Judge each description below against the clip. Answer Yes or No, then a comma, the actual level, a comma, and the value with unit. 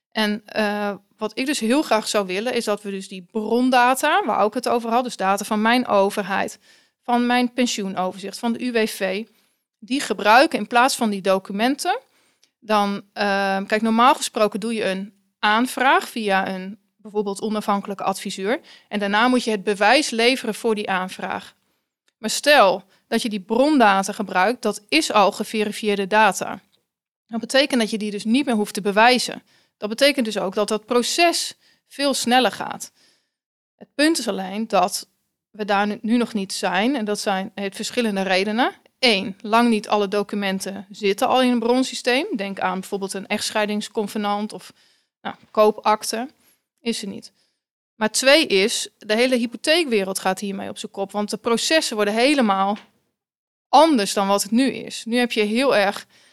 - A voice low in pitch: No, high, 215 Hz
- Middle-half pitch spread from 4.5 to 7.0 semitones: No, average, 3.2 semitones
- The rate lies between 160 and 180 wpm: Yes, average, 170 wpm